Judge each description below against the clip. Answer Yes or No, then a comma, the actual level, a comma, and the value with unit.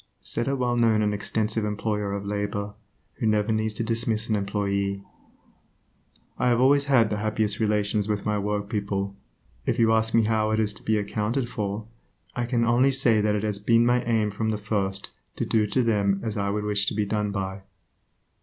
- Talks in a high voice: No, low, 105 Hz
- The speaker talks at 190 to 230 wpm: Yes, average, 200 wpm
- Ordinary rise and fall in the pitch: No, narrow, 1.9 semitones